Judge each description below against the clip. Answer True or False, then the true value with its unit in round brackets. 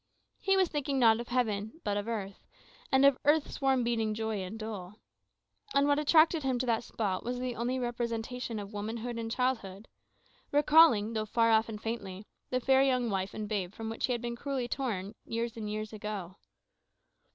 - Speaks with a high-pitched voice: True (230 Hz)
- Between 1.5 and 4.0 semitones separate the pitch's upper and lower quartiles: True (3.2 semitones)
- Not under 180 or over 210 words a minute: True (190 wpm)